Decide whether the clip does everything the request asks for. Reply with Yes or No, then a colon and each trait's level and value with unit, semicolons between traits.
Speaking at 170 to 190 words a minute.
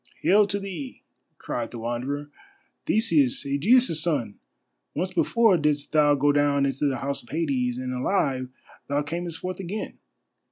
No: average, 150 wpm